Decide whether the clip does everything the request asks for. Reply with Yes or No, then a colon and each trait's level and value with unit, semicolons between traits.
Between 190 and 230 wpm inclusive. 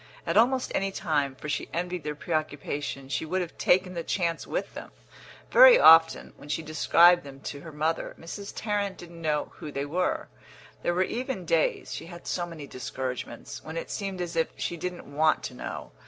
Yes: average, 195 wpm